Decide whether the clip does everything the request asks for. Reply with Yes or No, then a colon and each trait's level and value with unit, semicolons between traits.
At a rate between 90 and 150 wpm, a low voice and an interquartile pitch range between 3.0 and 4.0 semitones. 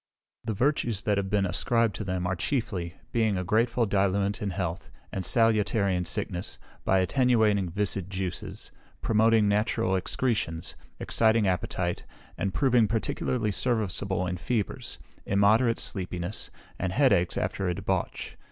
Yes: average, 140 wpm; low, 100 Hz; average, 3.5 semitones